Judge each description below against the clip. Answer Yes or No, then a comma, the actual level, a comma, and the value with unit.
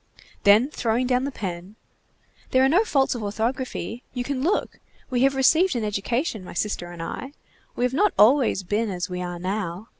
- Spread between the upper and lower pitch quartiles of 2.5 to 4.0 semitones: No, average, 5.1 semitones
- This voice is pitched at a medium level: No, high, 235 Hz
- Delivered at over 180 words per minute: Yes, average, 190 wpm